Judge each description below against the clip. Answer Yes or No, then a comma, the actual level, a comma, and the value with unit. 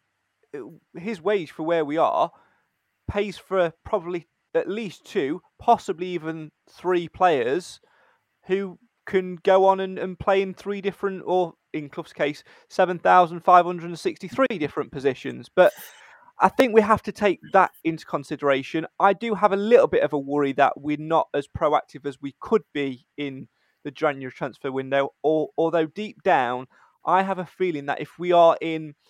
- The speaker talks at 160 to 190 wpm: Yes, average, 165 wpm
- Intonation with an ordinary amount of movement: Yes, average, 4.6 semitones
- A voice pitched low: No, medium, 175 Hz